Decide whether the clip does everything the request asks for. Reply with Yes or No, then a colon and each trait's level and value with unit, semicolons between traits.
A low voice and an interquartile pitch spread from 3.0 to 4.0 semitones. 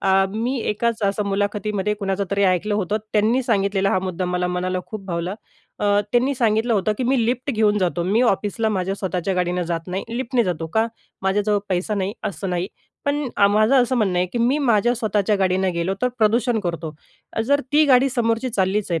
No: high, 205 Hz; average, 3.6 semitones